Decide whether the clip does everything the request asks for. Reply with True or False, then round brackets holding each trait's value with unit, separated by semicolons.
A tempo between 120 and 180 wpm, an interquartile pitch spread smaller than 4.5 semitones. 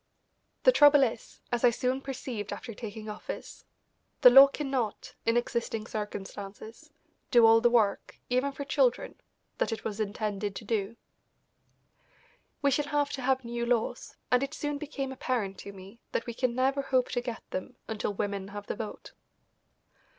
True (165 wpm; 4.0 semitones)